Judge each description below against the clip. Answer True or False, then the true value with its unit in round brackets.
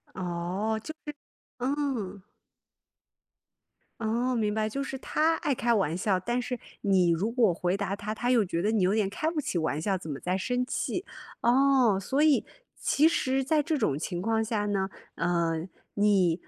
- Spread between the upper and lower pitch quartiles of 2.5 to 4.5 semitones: False (5.6 semitones)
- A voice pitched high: True (215 Hz)